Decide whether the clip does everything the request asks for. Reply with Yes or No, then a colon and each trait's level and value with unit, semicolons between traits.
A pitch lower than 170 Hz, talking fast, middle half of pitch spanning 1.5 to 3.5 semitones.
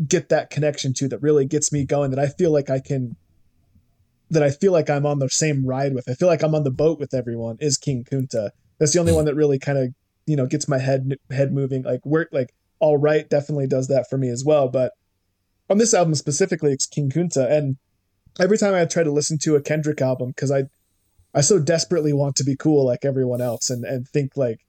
Yes: medium, 140 Hz; fast, 240 wpm; average, 2.8 semitones